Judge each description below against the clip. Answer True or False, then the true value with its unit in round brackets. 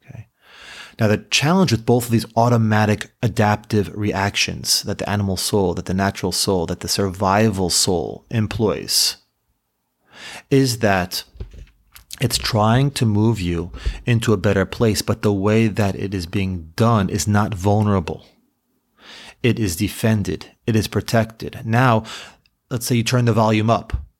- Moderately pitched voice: False (105 Hz)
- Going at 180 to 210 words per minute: False (145 wpm)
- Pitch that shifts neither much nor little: True (3.1 semitones)